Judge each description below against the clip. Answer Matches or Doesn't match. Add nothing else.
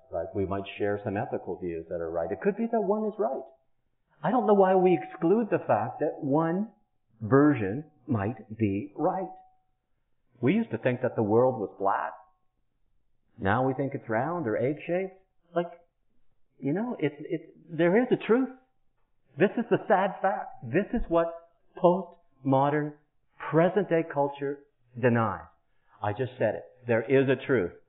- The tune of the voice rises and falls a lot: Matches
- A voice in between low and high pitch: Matches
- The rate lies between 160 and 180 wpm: Matches